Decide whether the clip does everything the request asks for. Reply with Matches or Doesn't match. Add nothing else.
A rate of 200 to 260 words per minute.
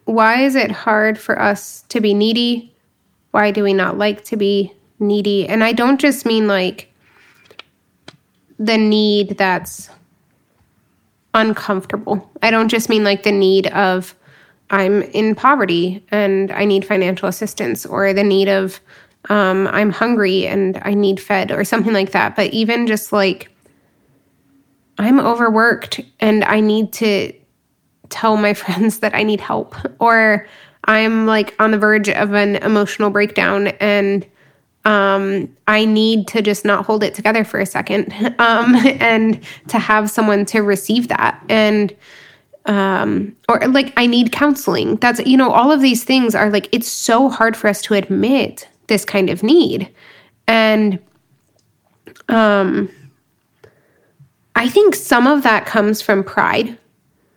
Doesn't match